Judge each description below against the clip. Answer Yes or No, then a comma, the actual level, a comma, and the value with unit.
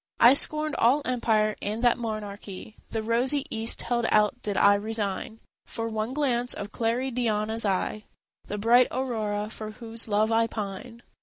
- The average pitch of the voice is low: No, high, 225 Hz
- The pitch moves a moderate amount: No, narrow, 2.3 semitones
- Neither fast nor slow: Yes, average, 155 wpm